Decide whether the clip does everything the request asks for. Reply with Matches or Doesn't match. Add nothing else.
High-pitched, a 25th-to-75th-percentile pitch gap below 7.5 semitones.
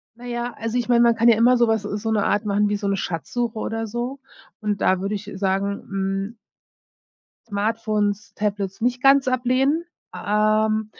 Matches